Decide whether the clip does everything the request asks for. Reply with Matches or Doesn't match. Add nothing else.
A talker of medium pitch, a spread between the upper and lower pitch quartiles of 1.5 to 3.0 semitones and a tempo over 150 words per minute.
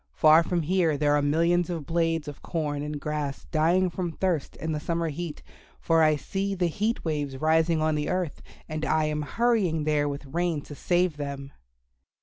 Matches